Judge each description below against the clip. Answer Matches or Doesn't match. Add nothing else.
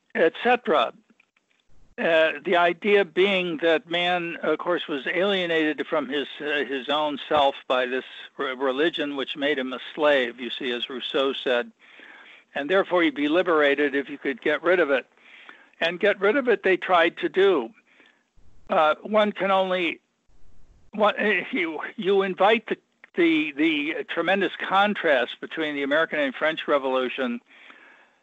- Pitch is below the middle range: Doesn't match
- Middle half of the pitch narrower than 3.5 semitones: Doesn't match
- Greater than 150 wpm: Doesn't match